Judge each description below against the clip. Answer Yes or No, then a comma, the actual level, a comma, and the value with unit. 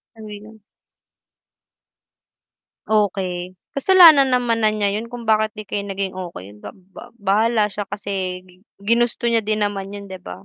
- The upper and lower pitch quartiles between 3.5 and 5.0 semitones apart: No, average, 2.7 semitones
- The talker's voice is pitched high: Yes, high, 210 Hz